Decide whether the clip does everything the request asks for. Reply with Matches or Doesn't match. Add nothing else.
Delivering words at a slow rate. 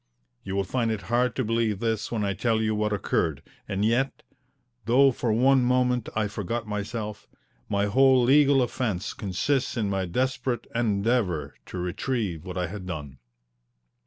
Doesn't match